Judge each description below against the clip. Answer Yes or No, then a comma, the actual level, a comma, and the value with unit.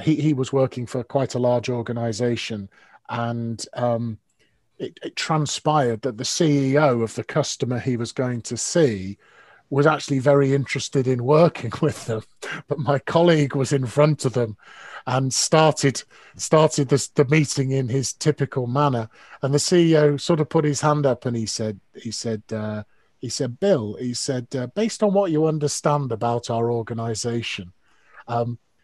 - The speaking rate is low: No, average, 165 wpm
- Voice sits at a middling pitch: No, low, 130 Hz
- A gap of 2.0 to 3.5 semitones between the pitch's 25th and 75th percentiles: No, average, 4.0 semitones